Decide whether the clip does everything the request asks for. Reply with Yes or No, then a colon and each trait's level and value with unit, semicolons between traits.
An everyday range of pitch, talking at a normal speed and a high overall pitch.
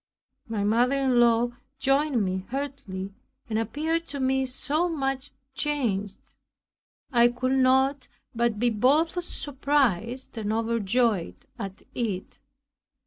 No: average, 3.7 semitones; slow, 115 wpm; very high, 250 Hz